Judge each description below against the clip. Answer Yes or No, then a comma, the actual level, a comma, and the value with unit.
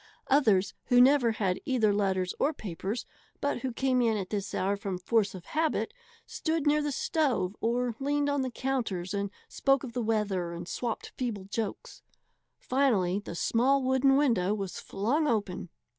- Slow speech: No, average, 170 wpm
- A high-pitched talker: Yes, high, 230 Hz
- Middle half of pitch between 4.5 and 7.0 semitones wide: Yes, wide, 5.5 semitones